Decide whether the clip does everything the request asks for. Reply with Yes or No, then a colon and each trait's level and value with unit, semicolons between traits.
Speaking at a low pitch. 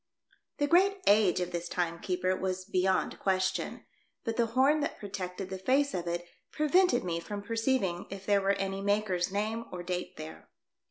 No: high, 195 Hz